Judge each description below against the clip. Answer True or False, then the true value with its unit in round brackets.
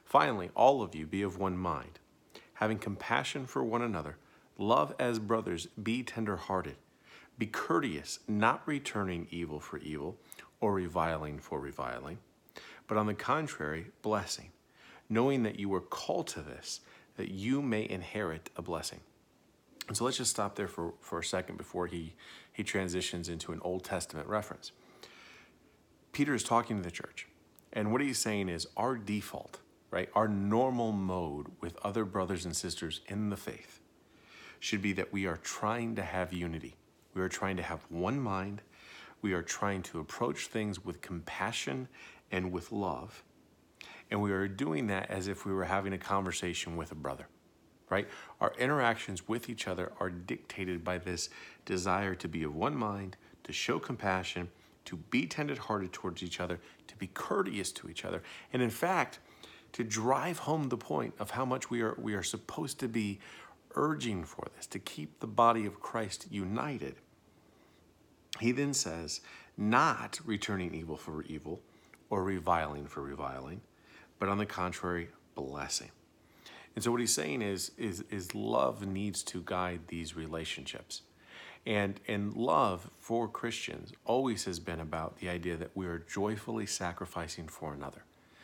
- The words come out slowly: False (165 wpm)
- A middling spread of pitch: True (3.9 semitones)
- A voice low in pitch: True (95 Hz)